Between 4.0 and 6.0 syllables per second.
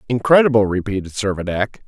No: 6.2 syllables/s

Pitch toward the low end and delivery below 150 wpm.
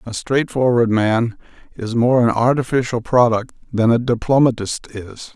Yes: low, 120 Hz; slow, 135 wpm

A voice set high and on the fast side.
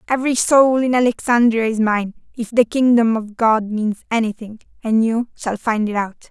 No: high, 225 Hz; average, 180 wpm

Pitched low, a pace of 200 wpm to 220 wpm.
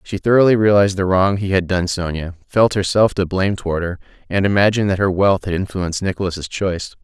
Yes: very low, 95 Hz; fast, 205 wpm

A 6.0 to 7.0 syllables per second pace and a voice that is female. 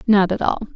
Yes: 6.4 syllables/s; female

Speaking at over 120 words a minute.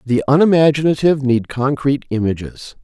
No: slow, 105 wpm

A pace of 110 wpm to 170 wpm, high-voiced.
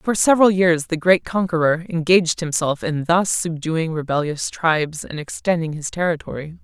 No: average, 155 wpm; medium, 165 Hz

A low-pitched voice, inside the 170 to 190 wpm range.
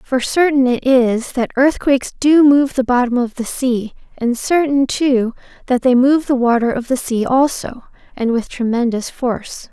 No: very high, 255 Hz; average, 180 wpm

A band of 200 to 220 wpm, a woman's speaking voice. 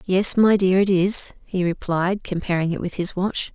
Yes: fast, 205 wpm; female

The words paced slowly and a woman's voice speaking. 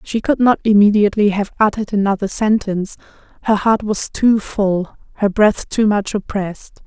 No: average, 155 wpm; female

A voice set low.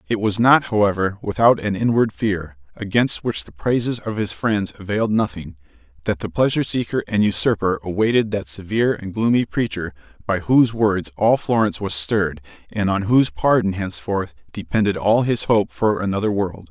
Yes: low, 100 Hz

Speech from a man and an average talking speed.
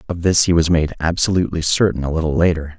No: male; fast, 215 wpm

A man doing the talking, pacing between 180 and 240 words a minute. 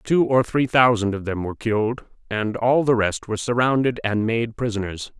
Yes: male; average, 195 wpm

